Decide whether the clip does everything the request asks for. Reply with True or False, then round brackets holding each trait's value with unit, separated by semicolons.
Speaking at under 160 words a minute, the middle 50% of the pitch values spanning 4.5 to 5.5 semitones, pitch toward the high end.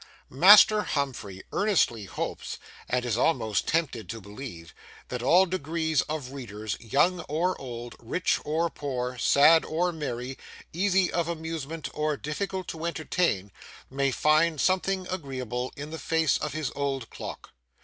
False (140 wpm; 5.2 semitones; 150 Hz)